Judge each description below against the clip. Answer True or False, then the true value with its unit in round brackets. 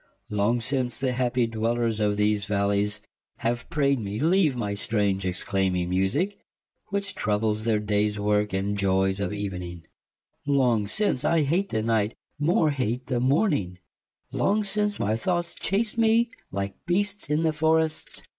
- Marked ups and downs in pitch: True (7.2 semitones)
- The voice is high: False (115 Hz)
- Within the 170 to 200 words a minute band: False (150 wpm)